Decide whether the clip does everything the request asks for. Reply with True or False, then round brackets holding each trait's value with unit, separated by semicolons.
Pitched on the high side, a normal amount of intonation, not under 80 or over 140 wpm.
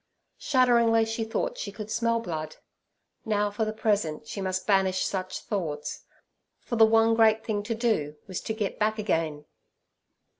False (215 Hz; 3.1 semitones; 160 wpm)